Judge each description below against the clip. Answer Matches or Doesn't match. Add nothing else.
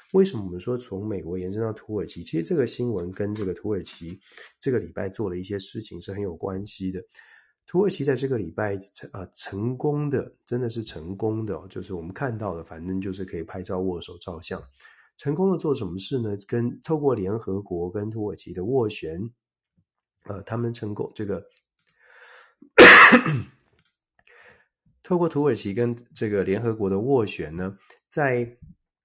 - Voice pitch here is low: Matches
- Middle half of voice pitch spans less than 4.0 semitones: Doesn't match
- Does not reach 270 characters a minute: Matches